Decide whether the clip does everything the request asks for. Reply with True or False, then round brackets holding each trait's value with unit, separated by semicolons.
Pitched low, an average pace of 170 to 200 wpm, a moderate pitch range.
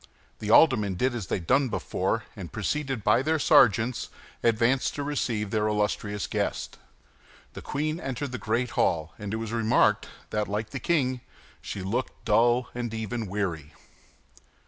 False (115 Hz; 160 wpm; 3.5 semitones)